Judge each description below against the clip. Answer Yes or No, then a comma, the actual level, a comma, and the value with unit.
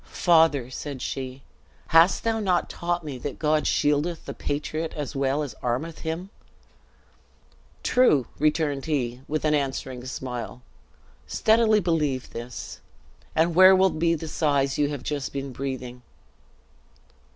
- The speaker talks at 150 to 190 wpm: No, slow, 135 wpm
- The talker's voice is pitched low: No, medium, 150 Hz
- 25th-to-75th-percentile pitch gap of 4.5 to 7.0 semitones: No, average, 3.7 semitones